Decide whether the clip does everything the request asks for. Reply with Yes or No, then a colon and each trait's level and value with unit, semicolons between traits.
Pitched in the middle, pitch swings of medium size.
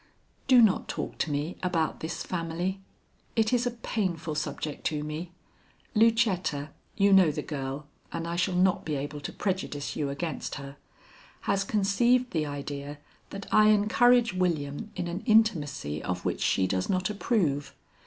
No: medium, 175 Hz; wide, 5.8 semitones